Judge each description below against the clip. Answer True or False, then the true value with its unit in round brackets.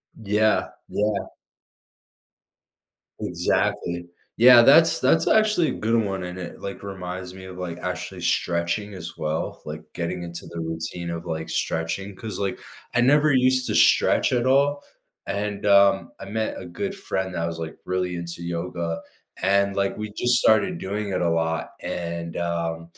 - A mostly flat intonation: False (4.2 semitones)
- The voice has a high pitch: False (95 Hz)